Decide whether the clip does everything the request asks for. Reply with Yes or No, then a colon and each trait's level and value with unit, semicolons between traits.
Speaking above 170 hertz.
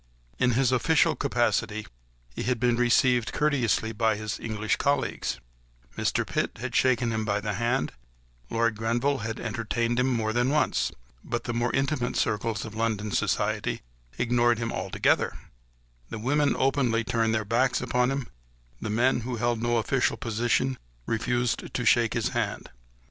No: low, 120 Hz